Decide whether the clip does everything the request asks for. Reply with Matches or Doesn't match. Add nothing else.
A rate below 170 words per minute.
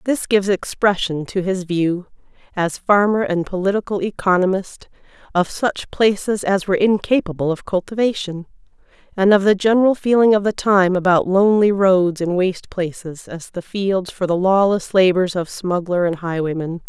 Matches